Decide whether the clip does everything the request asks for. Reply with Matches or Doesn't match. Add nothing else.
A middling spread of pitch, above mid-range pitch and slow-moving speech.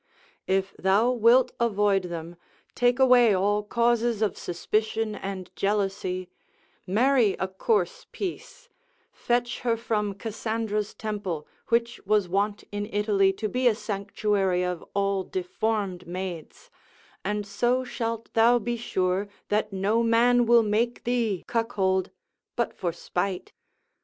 Matches